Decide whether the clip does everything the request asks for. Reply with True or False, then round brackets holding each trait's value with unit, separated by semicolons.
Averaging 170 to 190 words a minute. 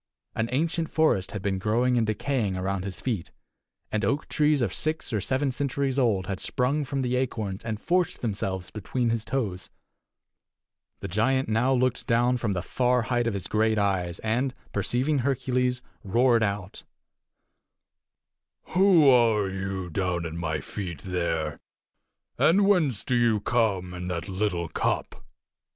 False (155 wpm)